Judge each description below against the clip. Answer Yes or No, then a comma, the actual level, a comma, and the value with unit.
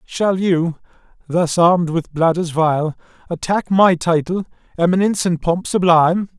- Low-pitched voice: No, medium, 175 Hz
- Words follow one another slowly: Yes, slow, 130 wpm